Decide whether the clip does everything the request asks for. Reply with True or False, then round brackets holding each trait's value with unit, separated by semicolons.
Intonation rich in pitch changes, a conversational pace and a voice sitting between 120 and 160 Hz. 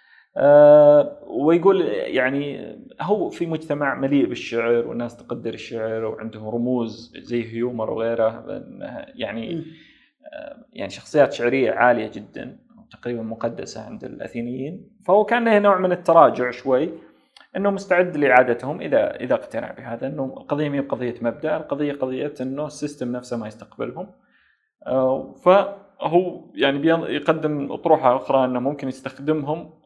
True (6.8 semitones; 115 wpm; 140 Hz)